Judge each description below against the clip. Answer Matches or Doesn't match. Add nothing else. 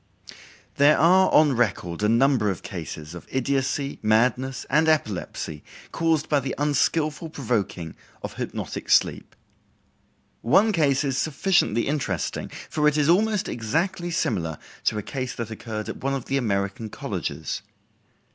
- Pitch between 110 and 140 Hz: Matches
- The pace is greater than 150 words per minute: Doesn't match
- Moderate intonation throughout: Doesn't match